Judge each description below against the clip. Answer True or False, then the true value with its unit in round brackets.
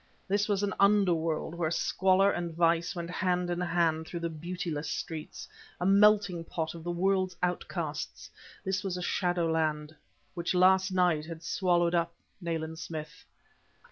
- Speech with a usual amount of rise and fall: False (2.1 semitones)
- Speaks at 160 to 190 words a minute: False (150 wpm)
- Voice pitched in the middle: True (175 Hz)